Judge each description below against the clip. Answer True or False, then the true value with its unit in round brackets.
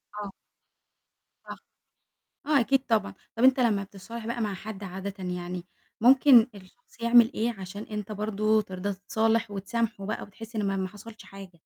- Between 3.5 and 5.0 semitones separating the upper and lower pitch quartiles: False (2.9 semitones)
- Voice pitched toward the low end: False (210 Hz)